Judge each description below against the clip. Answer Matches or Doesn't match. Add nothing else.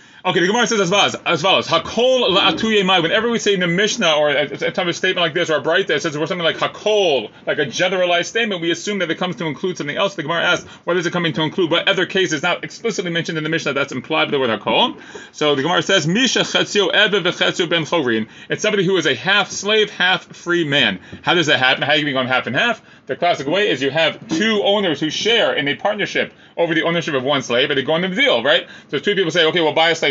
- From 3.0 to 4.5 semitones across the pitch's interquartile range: Matches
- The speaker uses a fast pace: Matches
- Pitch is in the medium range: Matches